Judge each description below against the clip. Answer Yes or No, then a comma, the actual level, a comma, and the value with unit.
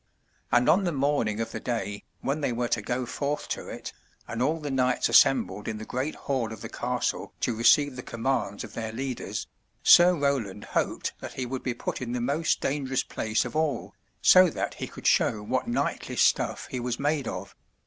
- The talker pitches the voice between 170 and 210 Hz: No, low, 125 Hz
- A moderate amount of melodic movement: Yes, average, 3.6 semitones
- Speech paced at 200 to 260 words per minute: Yes, fast, 205 wpm